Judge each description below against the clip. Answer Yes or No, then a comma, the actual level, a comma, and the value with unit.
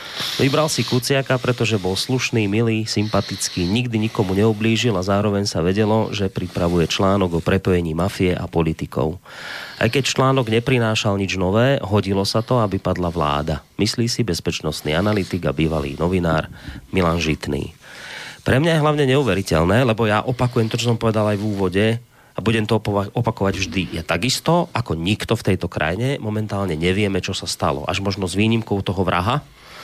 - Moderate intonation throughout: Yes, average, 4.1 semitones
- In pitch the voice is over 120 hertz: No, low, 105 Hz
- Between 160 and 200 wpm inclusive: Yes, fast, 165 wpm